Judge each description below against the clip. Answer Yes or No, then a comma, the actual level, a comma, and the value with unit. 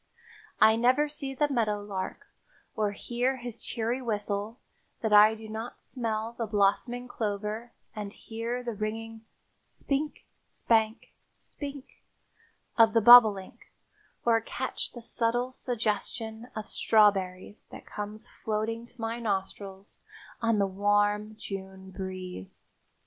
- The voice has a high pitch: Yes, high, 220 Hz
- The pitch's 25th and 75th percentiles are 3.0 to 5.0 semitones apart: No, narrow, 2.5 semitones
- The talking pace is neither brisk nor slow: No, slow, 120 wpm